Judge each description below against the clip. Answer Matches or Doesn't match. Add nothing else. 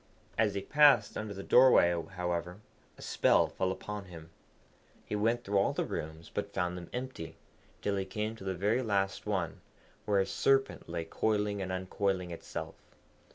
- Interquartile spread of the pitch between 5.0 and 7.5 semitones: Doesn't match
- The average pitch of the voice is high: Doesn't match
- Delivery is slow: Doesn't match